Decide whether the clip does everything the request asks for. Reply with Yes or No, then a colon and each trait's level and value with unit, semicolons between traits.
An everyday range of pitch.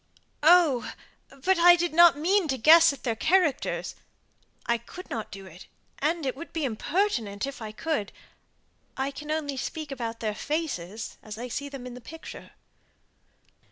No: wide, 5.8 semitones